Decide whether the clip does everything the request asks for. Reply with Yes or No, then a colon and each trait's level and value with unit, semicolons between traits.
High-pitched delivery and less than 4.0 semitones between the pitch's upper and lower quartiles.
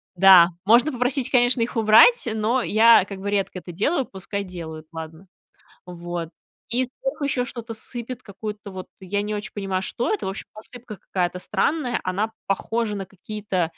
No: high, 210 Hz; average, 4.3 semitones